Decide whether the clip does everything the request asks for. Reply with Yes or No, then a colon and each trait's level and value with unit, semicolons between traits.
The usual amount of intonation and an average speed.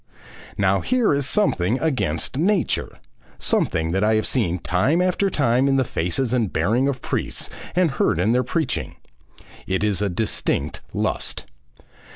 No: wide, 7.1 semitones; average, 155 wpm